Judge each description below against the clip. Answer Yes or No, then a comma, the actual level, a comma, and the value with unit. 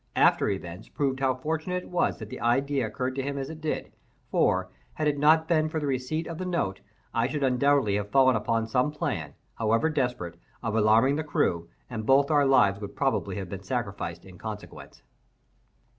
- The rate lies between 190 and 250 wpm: Yes, average, 200 wpm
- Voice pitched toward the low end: Yes, low, 130 Hz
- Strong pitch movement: Yes, wide, 5.7 semitones